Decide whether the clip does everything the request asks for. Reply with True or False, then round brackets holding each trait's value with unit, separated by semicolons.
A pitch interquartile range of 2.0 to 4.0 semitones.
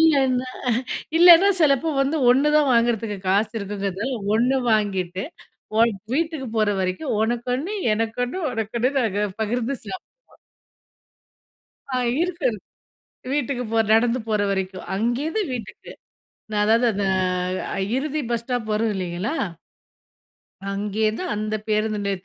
False (4.4 semitones)